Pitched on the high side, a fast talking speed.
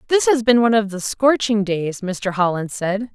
Yes: high, 210 Hz; fast, 210 wpm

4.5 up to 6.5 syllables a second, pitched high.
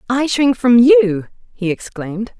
No: 4.1 syllables/s; high, 225 Hz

